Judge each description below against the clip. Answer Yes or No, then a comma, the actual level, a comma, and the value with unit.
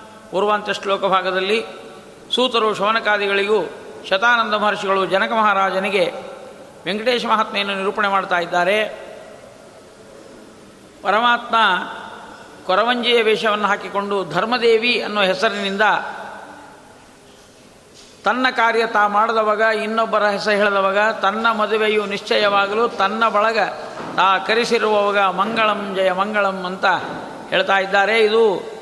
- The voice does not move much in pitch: Yes, narrow, 2.3 semitones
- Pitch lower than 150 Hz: No, high, 210 Hz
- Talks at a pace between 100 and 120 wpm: No, average, 85 wpm